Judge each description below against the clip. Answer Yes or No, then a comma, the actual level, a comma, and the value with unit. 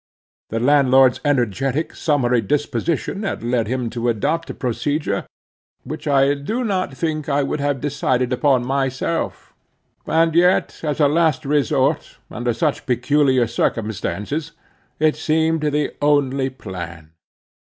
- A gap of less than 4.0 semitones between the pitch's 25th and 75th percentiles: Yes, average, 3.6 semitones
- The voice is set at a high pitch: No, medium, 140 Hz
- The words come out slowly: Yes, slow, 130 wpm